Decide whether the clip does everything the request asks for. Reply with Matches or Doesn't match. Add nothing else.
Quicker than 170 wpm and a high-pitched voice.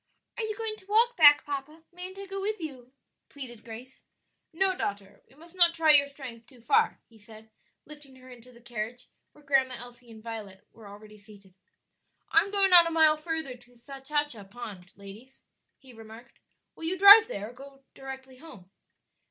Matches